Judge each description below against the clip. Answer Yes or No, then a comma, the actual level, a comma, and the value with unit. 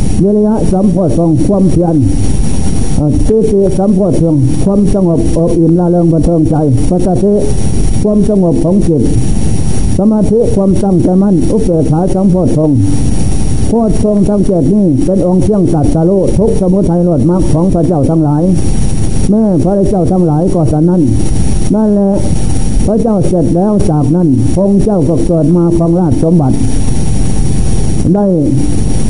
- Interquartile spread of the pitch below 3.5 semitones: No, average, 4.0 semitones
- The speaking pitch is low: No, medium, 175 Hz